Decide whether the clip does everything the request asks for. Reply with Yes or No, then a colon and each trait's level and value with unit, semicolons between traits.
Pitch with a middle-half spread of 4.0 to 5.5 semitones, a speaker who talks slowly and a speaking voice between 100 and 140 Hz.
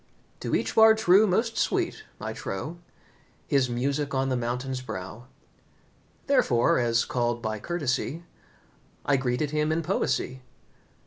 Yes: average, 5.1 semitones; slow, 130 wpm; low, 135 Hz